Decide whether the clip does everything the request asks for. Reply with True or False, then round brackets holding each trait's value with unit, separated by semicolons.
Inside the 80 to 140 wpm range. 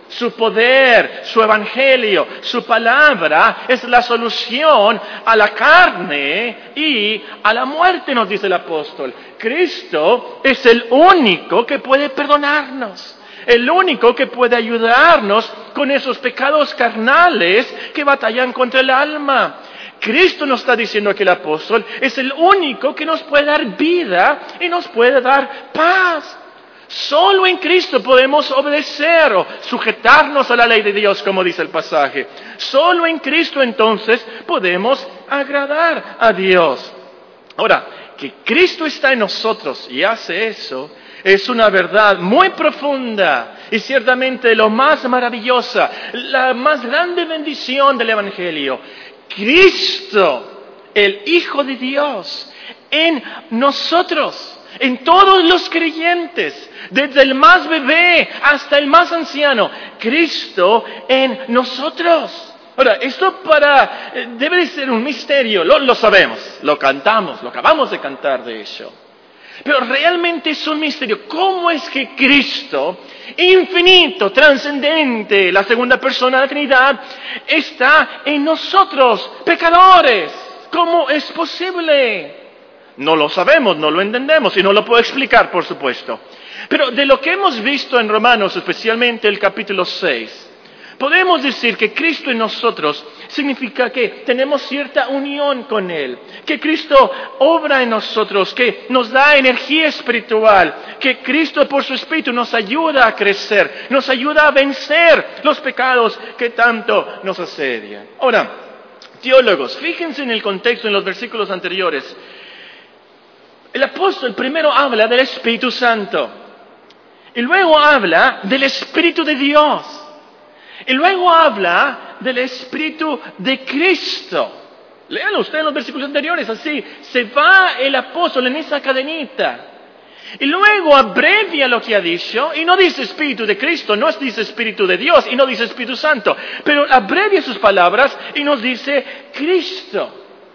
True (135 wpm)